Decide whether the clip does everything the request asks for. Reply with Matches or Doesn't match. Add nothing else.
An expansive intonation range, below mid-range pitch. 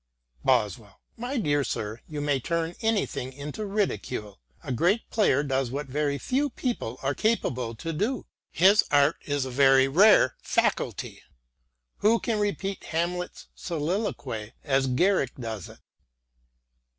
Doesn't match